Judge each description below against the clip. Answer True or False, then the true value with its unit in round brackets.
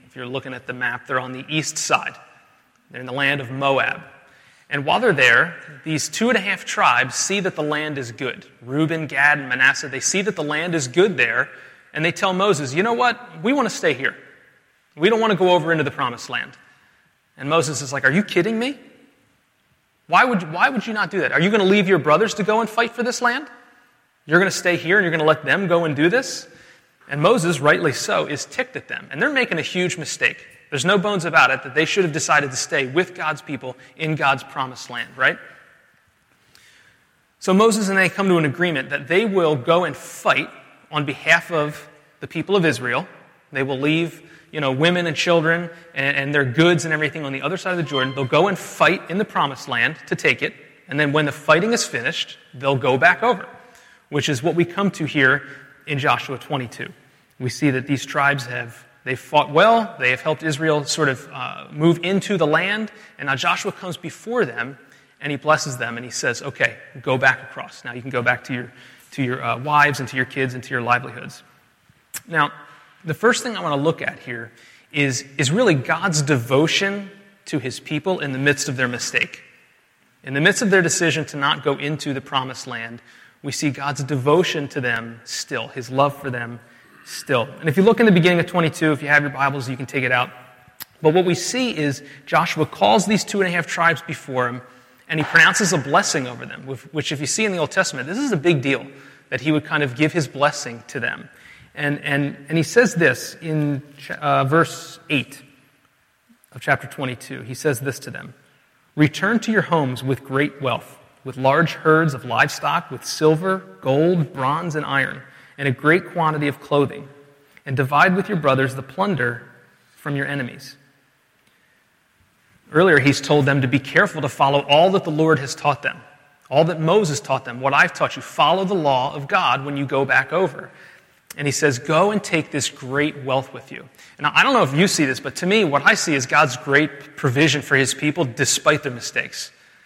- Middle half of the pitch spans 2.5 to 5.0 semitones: True (4.0 semitones)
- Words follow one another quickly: True (220 wpm)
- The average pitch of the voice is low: False (150 Hz)